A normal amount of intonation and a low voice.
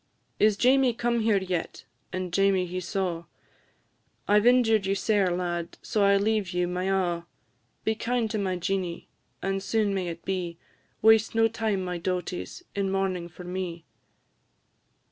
No: average, 3.2 semitones; high, 195 Hz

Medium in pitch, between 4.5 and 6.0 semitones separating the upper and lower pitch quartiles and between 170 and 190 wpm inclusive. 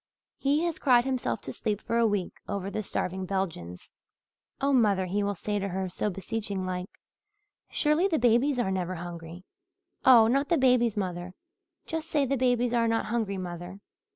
No: high, 210 Hz; average, 5.1 semitones; average, 180 wpm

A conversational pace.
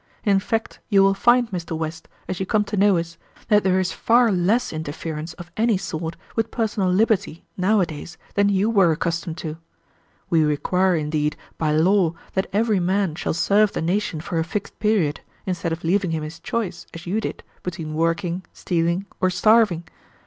Yes: average, 180 wpm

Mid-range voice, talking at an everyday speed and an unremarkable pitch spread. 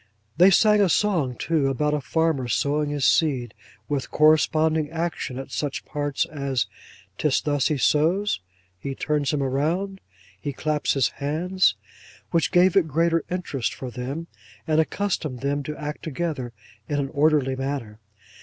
Yes: medium, 150 Hz; average, 155 wpm; average, 3.2 semitones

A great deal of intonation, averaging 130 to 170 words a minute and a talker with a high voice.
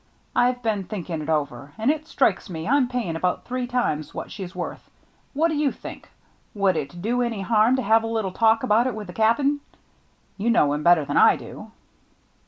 No: wide, 5.9 semitones; fast, 205 wpm; high, 220 Hz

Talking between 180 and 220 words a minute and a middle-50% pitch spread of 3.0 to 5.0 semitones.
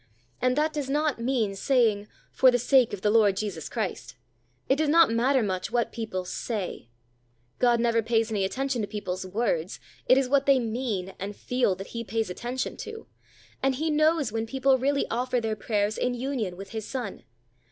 Yes: average, 190 wpm; average, 4.3 semitones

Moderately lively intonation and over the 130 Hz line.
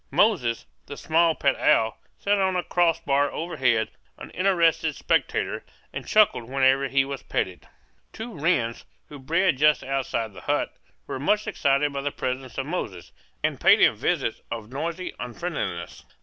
Yes: average, 4.8 semitones; medium, 140 Hz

